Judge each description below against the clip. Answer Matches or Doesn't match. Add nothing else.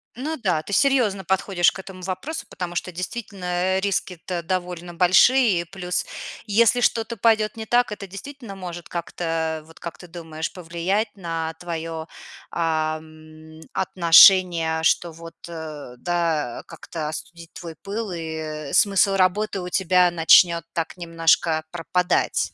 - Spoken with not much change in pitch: Doesn't match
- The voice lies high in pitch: Doesn't match